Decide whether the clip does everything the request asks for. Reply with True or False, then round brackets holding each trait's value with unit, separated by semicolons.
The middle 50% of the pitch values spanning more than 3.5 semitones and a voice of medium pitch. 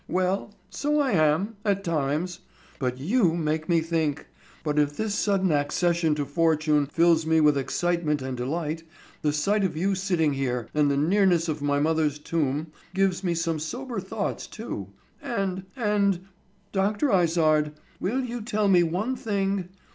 True (4.5 semitones; 170 Hz)